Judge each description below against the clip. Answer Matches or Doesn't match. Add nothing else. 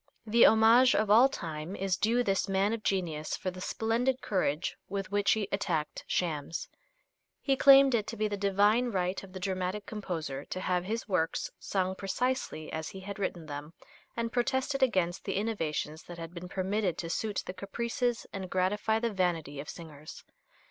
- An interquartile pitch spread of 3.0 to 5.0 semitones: Matches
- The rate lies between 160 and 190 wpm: Matches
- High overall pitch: Matches